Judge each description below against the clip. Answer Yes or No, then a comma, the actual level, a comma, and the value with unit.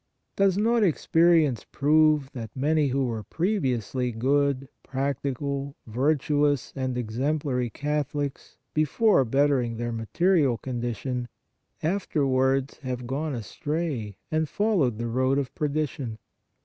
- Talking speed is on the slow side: Yes, slow, 110 wpm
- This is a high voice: No, medium, 140 Hz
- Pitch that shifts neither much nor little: Yes, average, 3.6 semitones